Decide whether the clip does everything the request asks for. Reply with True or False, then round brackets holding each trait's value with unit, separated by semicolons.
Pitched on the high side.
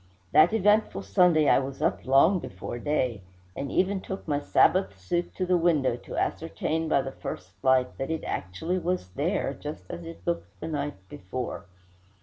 False (140 Hz)